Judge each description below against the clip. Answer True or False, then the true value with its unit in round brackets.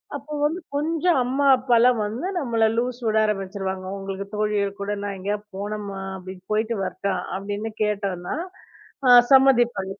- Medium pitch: False (210 Hz)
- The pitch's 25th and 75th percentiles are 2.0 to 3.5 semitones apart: False (3.9 semitones)